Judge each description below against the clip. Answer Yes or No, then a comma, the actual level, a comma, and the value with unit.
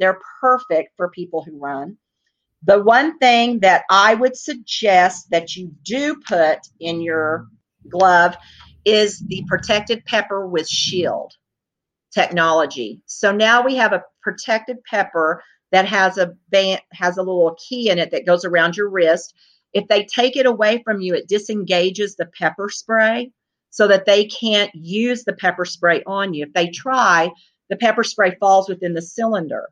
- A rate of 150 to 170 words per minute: Yes, average, 165 wpm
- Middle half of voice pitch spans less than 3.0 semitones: No, average, 4.1 semitones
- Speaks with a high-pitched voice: Yes, high, 195 Hz